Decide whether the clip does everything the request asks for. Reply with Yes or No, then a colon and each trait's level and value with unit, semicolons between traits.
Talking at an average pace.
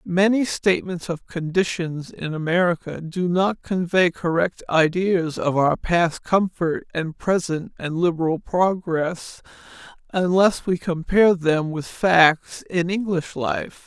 No: slow, 125 wpm